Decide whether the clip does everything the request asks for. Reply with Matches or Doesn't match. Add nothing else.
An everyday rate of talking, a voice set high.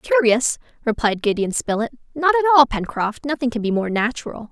Matches